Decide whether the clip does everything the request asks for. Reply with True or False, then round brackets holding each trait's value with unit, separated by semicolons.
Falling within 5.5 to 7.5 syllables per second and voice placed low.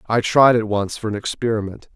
True (5.8 syllables/s; 110 Hz)